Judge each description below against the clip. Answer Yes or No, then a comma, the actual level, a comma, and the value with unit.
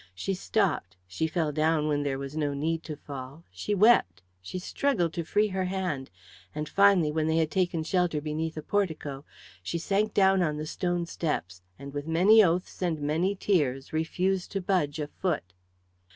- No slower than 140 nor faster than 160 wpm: No, average, 180 wpm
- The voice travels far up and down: No, average, 4.1 semitones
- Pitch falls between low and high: Yes, medium, 160 Hz